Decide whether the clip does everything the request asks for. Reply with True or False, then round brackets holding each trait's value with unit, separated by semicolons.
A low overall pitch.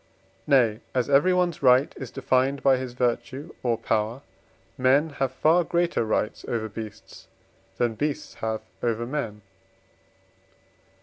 True (130 Hz)